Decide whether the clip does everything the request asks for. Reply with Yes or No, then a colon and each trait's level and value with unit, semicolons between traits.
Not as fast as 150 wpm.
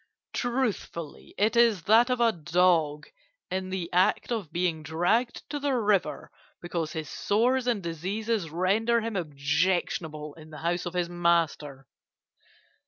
Yes: average, 140 wpm